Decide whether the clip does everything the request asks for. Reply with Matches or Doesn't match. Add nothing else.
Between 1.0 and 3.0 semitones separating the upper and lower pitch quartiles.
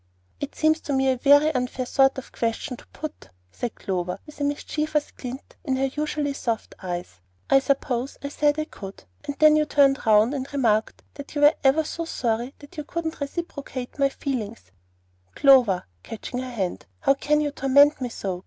Doesn't match